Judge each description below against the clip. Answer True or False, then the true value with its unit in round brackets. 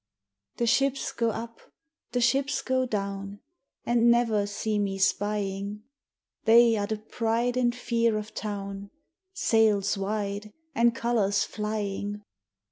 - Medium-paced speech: False (125 wpm)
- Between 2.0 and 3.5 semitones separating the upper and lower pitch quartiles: True (2.6 semitones)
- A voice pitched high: True (215 Hz)